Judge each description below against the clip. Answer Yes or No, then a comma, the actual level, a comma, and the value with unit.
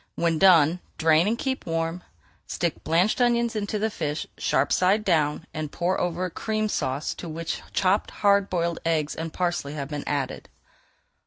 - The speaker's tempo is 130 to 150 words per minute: No, average, 170 wpm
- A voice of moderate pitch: Yes, medium, 170 Hz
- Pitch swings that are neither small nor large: Yes, average, 4.3 semitones